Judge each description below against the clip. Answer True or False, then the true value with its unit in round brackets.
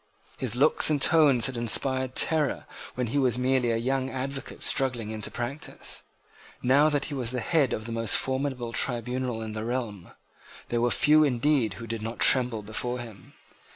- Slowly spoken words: False (185 wpm)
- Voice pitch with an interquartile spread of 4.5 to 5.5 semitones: False (2.8 semitones)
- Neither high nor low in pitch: False (125 Hz)